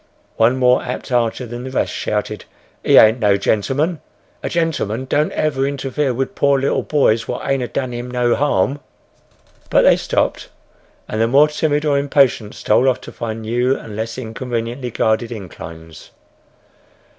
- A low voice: Yes, low, 125 Hz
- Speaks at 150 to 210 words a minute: Yes, average, 160 wpm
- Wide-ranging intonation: No, average, 3.5 semitones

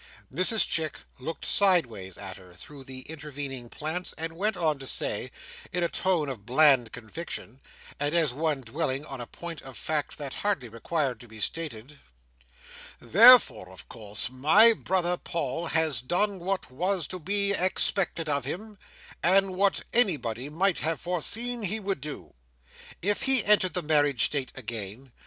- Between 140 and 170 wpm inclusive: Yes, average, 160 wpm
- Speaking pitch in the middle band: Yes, medium, 155 Hz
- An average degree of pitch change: No, wide, 6.1 semitones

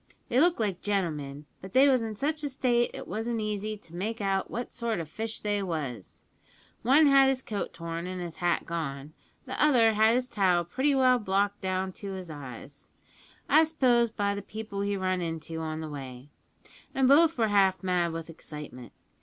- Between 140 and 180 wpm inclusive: No, average, 195 wpm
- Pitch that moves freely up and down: Yes, wide, 6.1 semitones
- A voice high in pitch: Yes, high, 200 Hz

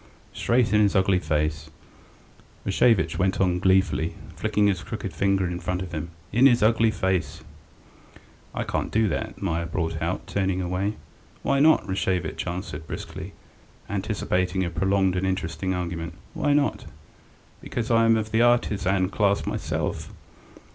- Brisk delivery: No, average, 145 wpm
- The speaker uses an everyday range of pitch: Yes, average, 3.1 semitones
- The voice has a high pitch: No, very low, 95 Hz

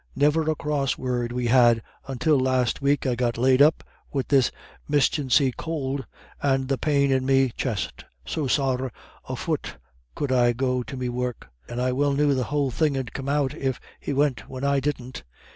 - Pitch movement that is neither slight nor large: No, narrow, 2.1 semitones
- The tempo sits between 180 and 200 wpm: Yes, average, 190 wpm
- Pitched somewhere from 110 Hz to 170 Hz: Yes, low, 135 Hz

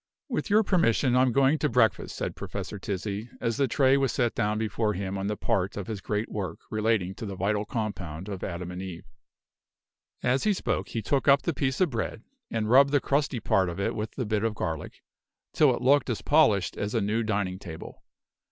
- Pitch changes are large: No, average, 4.9 semitones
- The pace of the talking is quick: Yes, fast, 215 wpm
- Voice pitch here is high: No, low, 110 Hz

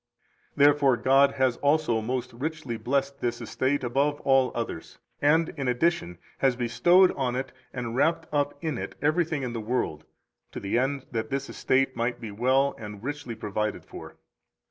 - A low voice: Yes, low, 130 Hz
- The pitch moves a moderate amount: Yes, average, 3.2 semitones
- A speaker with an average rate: Yes, average, 170 wpm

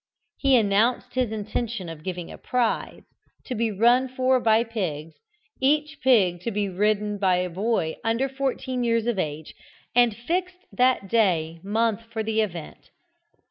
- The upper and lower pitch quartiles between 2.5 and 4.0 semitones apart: No, average, 4.6 semitones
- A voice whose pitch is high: Yes, high, 225 Hz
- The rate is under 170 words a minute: Yes, average, 155 wpm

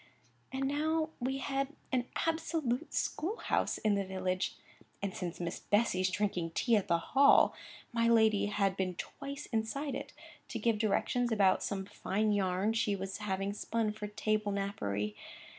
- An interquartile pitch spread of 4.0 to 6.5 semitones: Yes, average, 4.5 semitones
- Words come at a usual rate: Yes, average, 160 wpm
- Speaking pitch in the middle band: No, high, 210 Hz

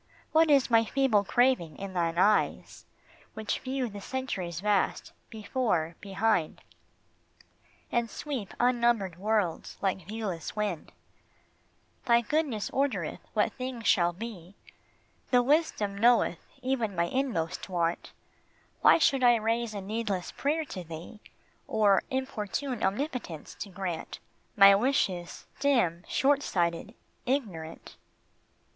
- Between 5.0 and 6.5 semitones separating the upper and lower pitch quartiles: Yes, wide, 5.5 semitones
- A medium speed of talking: No, slow, 115 wpm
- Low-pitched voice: No, high, 215 Hz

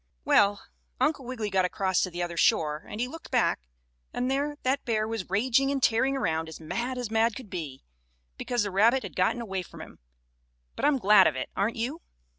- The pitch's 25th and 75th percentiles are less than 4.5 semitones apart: No, wide, 5.4 semitones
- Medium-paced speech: No, fast, 210 wpm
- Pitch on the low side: No, high, 220 Hz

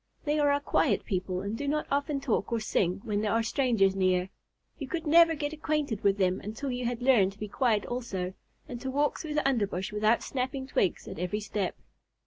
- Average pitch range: No, wide, 6.1 semitones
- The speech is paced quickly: Yes, fast, 215 wpm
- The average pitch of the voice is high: Yes, high, 235 Hz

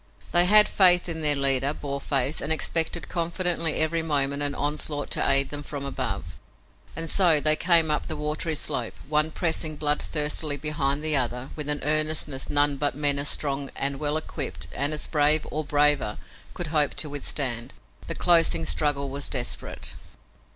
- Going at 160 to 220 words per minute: Yes, average, 170 wpm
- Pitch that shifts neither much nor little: No, narrow, 2.0 semitones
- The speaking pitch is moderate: Yes, medium, 150 Hz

